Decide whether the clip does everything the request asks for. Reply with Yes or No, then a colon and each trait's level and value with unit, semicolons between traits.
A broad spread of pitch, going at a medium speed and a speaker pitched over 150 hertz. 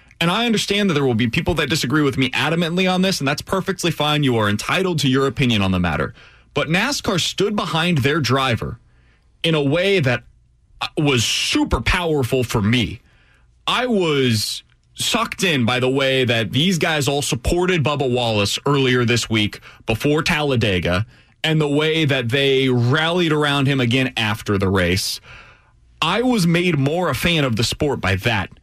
No: wide, 6.1 semitones; average, 180 wpm; medium, 140 Hz